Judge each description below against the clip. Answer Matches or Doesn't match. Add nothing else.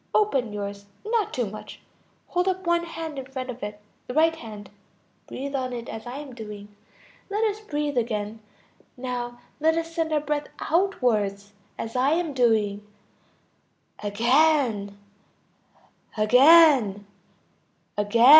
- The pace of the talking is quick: Doesn't match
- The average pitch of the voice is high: Matches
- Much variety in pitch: Matches